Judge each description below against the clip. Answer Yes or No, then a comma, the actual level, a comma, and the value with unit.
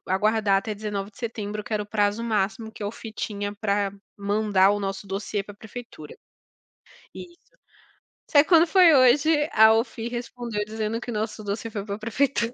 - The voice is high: Yes, high, 215 Hz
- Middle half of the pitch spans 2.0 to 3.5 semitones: Yes, narrow, 2.4 semitones